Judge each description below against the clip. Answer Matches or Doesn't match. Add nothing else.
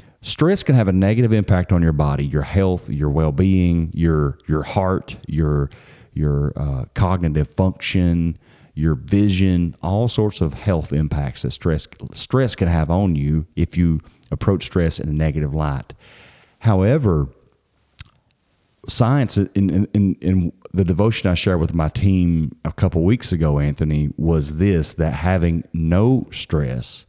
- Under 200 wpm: Matches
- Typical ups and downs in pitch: Matches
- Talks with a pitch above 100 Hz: Doesn't match